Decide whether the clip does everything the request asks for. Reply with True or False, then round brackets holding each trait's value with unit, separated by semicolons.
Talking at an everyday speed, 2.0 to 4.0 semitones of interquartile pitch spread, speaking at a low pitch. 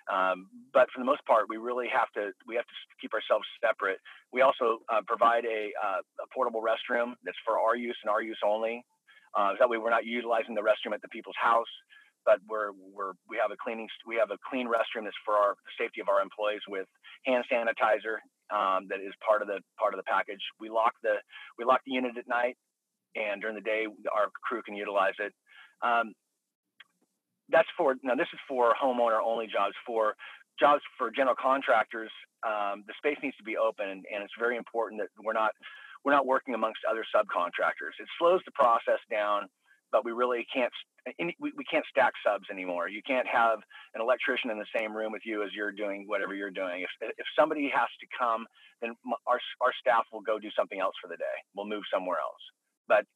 False (210 wpm; 2.6 semitones; 115 Hz)